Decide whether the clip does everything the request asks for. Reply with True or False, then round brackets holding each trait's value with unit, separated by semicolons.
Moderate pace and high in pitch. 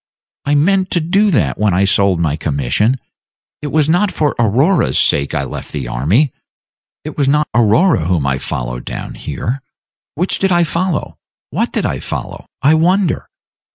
False (170 wpm; 140 Hz)